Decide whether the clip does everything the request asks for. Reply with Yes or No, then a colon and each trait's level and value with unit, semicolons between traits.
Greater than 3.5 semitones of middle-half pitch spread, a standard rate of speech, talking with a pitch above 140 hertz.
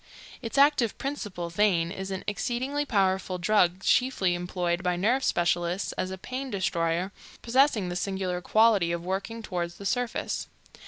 Yes: average, 4.6 semitones; average, 150 wpm; high, 190 Hz